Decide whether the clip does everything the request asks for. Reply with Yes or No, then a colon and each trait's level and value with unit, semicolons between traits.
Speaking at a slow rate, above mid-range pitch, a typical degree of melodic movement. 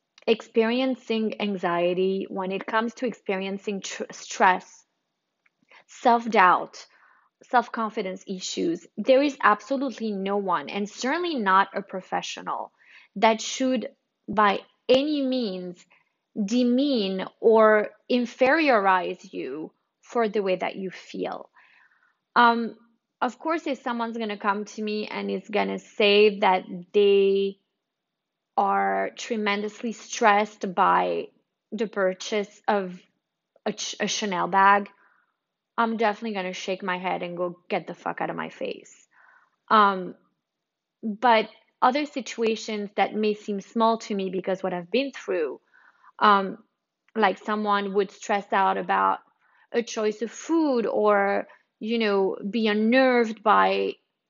Yes: slow, 125 wpm; high, 210 Hz; average, 3.4 semitones